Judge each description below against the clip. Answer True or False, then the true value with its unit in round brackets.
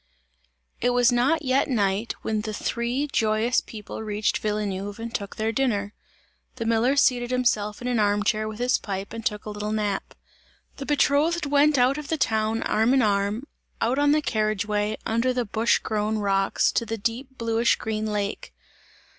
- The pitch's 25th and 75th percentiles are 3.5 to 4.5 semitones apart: False (3.1 semitones)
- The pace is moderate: True (180 wpm)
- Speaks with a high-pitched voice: True (225 Hz)